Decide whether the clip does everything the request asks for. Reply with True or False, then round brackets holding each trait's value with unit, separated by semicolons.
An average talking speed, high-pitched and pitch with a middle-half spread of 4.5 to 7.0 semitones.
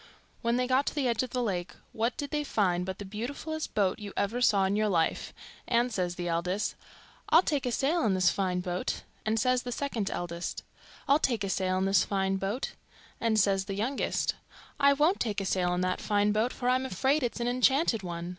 False (225 wpm; 215 Hz; 5.0 semitones)